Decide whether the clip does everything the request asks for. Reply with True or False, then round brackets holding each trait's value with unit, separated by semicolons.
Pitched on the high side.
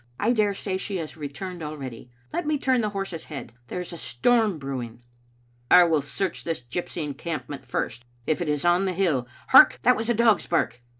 False (165 Hz)